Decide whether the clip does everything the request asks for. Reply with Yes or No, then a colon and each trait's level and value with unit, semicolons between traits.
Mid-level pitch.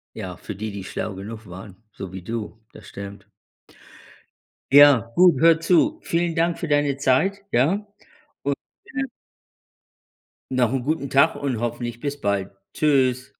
No: low, 130 Hz